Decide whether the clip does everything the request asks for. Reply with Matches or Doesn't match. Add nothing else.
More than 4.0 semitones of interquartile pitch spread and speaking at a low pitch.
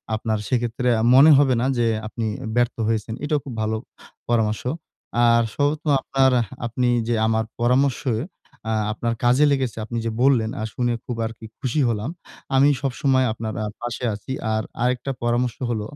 Doesn't match